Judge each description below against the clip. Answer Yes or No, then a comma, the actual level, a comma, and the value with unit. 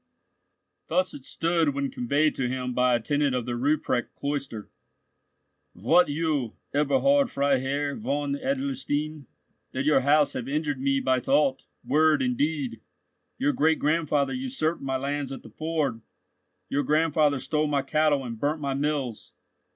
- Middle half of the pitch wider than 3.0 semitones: No, narrow, 2.6 semitones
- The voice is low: No, medium, 145 Hz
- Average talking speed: Yes, average, 150 wpm